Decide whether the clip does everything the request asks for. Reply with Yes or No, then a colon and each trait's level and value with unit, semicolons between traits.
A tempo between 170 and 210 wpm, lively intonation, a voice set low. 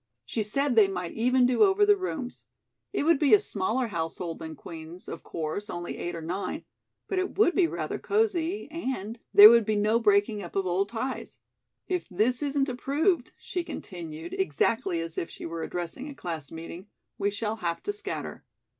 No: average, 190 wpm; wide, 8.6 semitones; high, 215 Hz